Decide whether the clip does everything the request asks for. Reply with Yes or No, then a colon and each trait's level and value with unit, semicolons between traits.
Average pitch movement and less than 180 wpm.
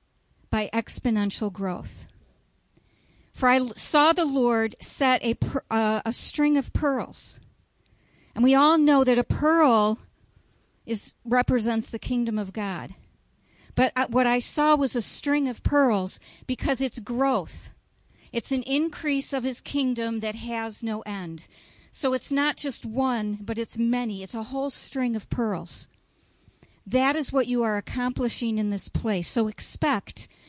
Yes: average, 3.3 semitones; average, 150 wpm